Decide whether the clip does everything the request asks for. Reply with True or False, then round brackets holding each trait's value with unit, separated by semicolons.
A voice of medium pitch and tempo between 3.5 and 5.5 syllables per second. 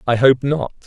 False (130 Hz; 4.9 syllables/s)